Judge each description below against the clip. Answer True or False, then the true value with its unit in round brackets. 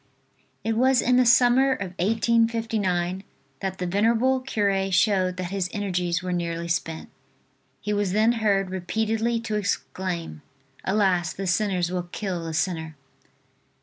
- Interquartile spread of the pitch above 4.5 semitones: False (3.8 semitones)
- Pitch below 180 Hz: False (195 Hz)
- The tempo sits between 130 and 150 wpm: True (140 wpm)